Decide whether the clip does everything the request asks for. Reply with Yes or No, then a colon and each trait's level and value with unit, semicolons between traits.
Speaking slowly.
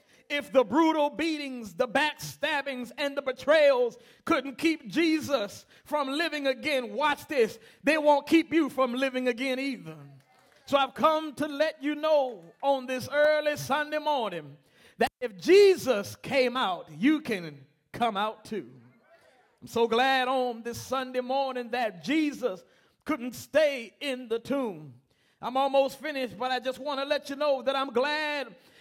No: average, 155 wpm